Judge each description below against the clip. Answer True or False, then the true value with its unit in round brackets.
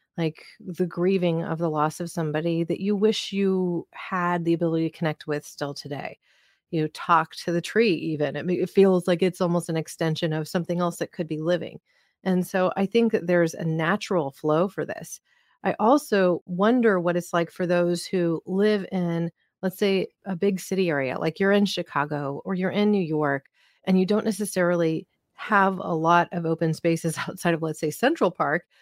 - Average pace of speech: True (195 wpm)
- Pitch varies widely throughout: False (2.6 semitones)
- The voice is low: False (175 Hz)